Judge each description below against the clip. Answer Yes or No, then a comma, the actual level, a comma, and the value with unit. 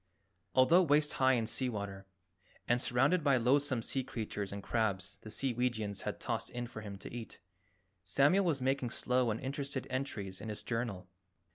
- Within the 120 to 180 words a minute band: Yes, average, 170 wpm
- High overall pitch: No, low, 120 Hz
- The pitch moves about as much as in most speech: Yes, average, 4.1 semitones